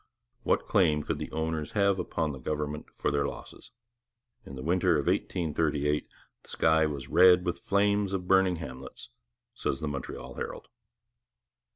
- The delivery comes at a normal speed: Yes, average, 160 wpm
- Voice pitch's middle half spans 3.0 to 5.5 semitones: Yes, average, 3.8 semitones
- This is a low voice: Yes, very low, 80 Hz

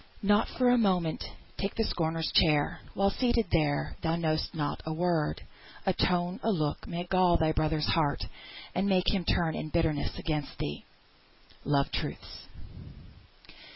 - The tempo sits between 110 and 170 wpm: Yes, average, 155 wpm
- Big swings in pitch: No, average, 3.4 semitones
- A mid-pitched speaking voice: Yes, medium, 170 Hz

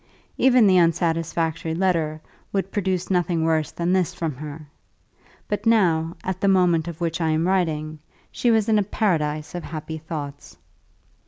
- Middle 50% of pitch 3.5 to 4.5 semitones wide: No, average, 2.8 semitones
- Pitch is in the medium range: Yes, medium, 170 Hz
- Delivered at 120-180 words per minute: Yes, average, 160 wpm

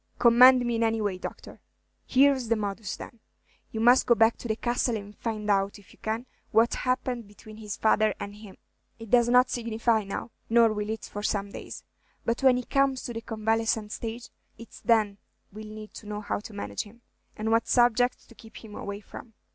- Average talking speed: No, fast, 210 wpm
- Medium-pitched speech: No, high, 225 Hz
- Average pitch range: No, narrow, 2.2 semitones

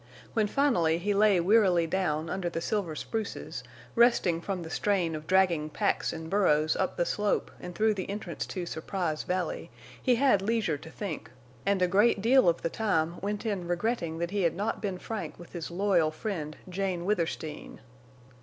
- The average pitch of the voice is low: No, medium, 185 Hz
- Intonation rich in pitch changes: No, average, 3.8 semitones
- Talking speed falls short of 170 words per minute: No, average, 180 wpm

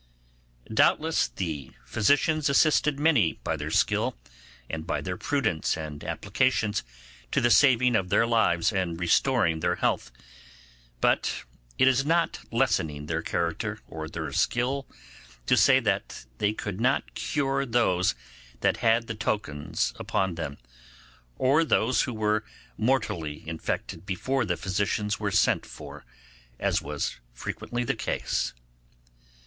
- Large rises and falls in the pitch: Yes, wide, 7.6 semitones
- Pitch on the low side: Yes, low, 105 Hz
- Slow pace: Yes, slow, 130 wpm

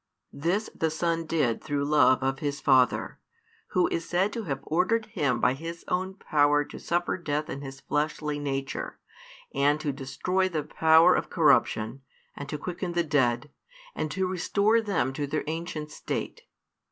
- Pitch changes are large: No, average, 3.7 semitones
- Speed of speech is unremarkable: Yes, average, 165 wpm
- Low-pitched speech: No, medium, 155 Hz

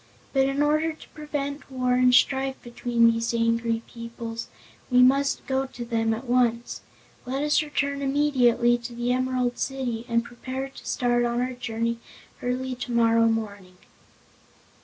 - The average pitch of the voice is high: Yes, high, 245 Hz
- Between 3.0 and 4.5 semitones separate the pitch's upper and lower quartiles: No, narrow, 2.4 semitones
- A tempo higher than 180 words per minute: No, average, 150 wpm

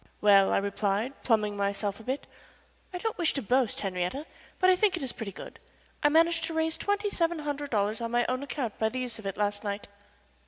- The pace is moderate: No, fast, 225 wpm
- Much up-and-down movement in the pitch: Yes, wide, 7.7 semitones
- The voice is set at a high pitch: Yes, high, 245 Hz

